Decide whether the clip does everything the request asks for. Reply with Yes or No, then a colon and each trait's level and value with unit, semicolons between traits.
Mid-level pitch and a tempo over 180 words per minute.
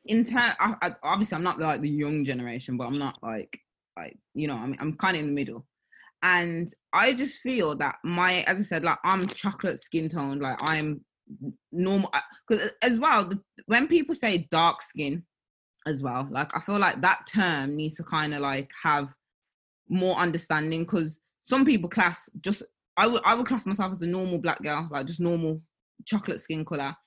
Yes: medium, 170 Hz; average, 200 wpm